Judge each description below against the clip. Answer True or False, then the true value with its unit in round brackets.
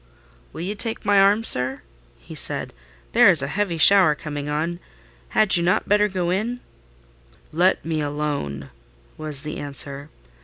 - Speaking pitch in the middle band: True (165 Hz)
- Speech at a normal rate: True (155 wpm)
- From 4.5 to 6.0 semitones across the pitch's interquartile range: True (5.1 semitones)